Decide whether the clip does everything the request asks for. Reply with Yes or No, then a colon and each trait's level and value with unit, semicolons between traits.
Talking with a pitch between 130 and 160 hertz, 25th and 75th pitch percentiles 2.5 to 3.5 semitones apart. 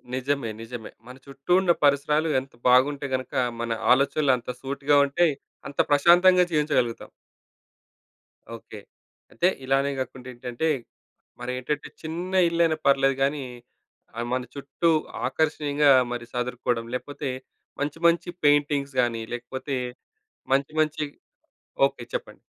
Yes: medium, 140 Hz; average, 2.9 semitones